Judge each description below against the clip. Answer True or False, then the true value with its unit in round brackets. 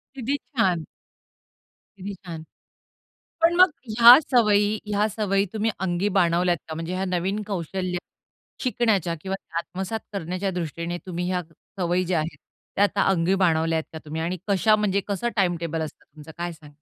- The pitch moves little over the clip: False (3.3 semitones)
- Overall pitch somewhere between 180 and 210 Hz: True (185 Hz)